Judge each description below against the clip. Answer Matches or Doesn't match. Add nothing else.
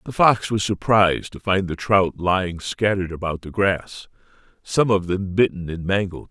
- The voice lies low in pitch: Matches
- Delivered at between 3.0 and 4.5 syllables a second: Doesn't match